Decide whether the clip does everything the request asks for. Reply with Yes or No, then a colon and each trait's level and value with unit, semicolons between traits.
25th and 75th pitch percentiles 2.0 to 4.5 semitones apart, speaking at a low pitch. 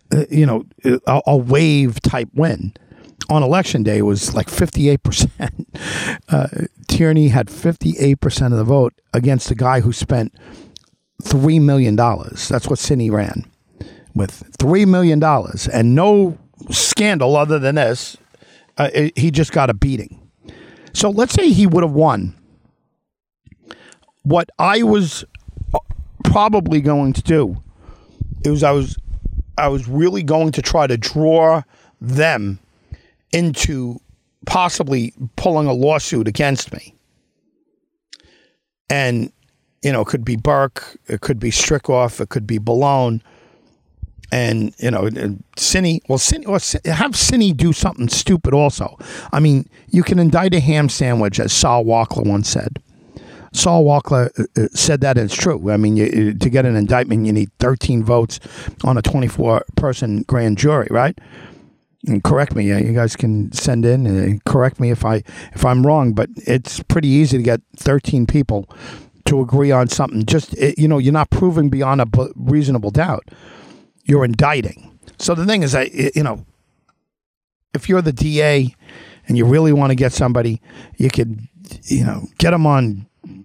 No: average, 4.9 semitones; low, 130 Hz